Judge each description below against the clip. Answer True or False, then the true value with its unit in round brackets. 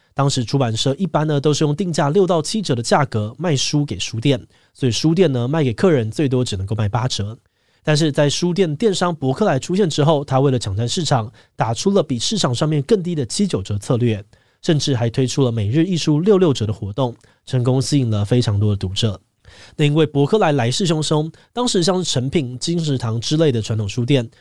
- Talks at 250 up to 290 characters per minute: False (325 characters per minute)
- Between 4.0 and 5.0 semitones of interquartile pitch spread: False (5.4 semitones)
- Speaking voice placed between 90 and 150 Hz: True (140 Hz)